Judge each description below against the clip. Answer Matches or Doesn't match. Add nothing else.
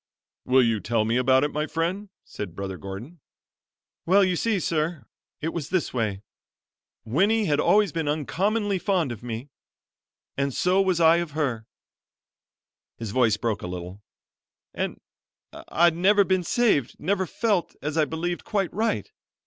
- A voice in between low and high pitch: Matches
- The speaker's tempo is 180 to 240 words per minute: Doesn't match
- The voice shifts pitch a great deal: Matches